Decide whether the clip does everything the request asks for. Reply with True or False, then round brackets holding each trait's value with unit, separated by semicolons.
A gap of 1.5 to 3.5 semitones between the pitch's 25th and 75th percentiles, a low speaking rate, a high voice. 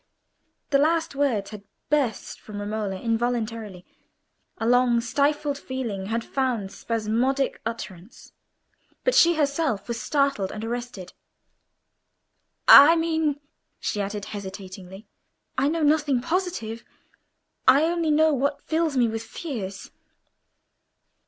False (5.5 semitones; 115 wpm; 245 Hz)